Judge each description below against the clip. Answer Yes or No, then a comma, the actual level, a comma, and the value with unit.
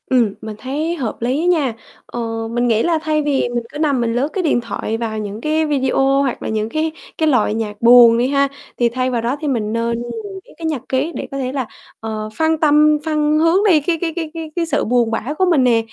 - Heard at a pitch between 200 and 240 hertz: No, very high, 265 Hz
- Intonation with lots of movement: No, average, 5.0 semitones